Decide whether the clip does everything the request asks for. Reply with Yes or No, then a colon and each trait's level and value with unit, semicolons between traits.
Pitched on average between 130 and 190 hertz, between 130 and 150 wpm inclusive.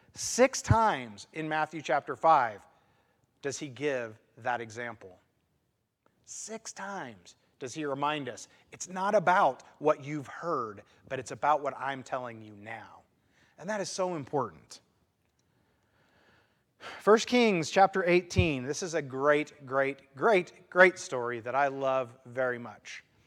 Yes: medium, 140 Hz; slow, 135 wpm